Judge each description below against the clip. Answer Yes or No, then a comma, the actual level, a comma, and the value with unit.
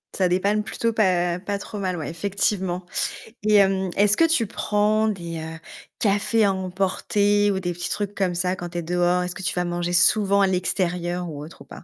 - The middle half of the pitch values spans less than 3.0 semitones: Yes, narrow, 2.6 semitones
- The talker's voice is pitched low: No, high, 190 Hz